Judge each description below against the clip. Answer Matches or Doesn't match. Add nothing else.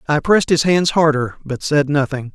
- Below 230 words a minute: Matches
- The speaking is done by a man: Matches